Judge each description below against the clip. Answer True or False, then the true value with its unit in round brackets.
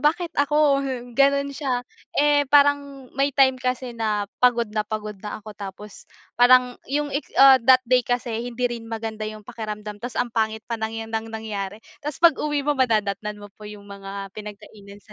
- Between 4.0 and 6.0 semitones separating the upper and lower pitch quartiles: True (4.3 semitones)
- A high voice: True (235 Hz)